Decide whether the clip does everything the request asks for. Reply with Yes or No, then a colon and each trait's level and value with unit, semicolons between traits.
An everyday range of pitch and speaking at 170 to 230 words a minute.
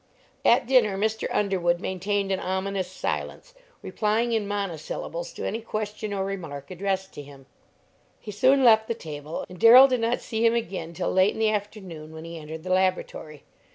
Yes: average, 4.1 semitones; average, 180 wpm